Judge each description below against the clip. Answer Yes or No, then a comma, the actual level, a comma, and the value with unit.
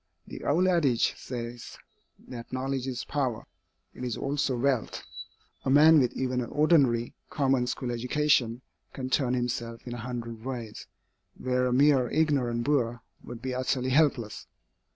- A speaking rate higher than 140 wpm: Yes, average, 150 wpm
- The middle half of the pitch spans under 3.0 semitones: Yes, narrow, 2.4 semitones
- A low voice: Yes, low, 125 Hz